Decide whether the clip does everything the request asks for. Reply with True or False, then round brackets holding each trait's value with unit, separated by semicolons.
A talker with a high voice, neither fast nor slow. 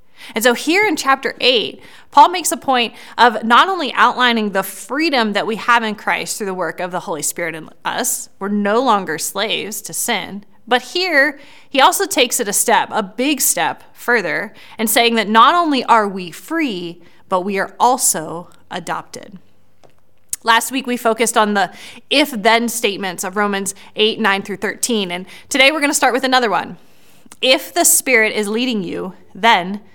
True (230 Hz; 185 wpm)